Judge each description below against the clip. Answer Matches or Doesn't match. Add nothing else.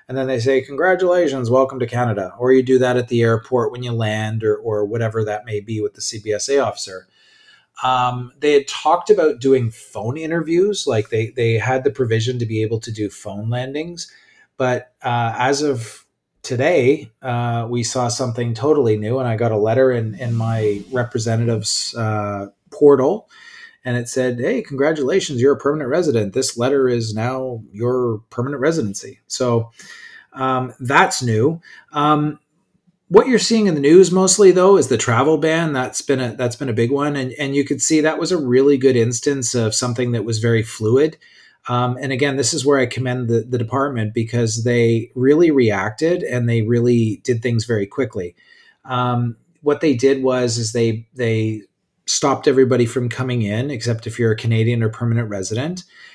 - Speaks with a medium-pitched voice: Doesn't match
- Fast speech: Doesn't match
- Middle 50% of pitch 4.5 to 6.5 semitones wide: Doesn't match